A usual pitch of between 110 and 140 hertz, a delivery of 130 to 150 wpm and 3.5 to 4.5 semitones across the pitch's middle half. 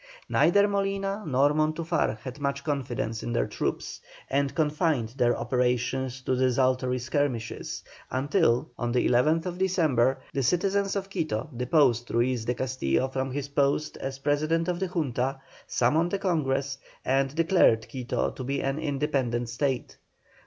Yes: low, 135 Hz; average, 145 wpm; average, 4.0 semitones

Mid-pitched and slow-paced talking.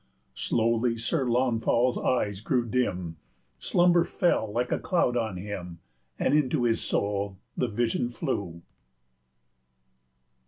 No: low, 115 Hz; slow, 120 wpm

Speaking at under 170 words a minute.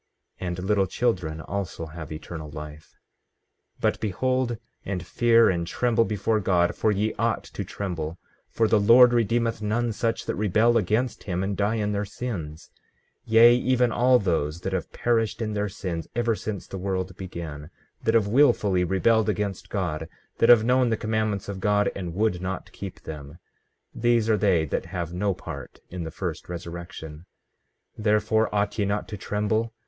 No: average, 175 wpm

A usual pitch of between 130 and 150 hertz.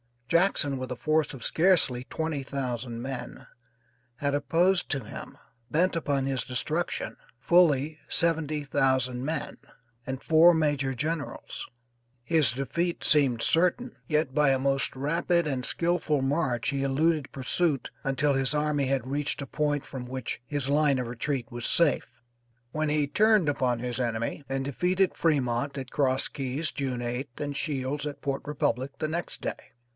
Yes: medium, 140 Hz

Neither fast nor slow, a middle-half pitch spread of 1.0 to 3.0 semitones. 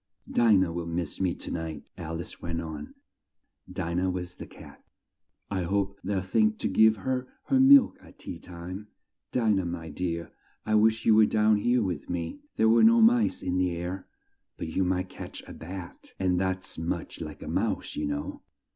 No: average, 195 wpm; average, 4.1 semitones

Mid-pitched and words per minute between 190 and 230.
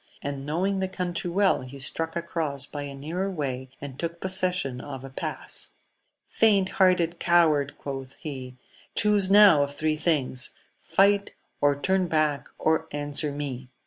No: medium, 155 Hz; average, 155 wpm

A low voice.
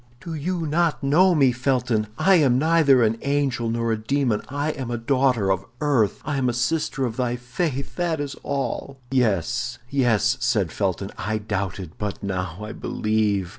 Yes: low, 125 Hz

